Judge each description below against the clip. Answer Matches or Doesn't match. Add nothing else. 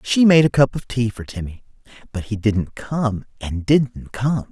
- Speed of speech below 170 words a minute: Doesn't match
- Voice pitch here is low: Matches